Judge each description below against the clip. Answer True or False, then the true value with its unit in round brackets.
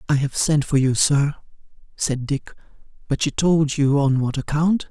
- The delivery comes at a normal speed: True (170 wpm)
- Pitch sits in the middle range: True (145 Hz)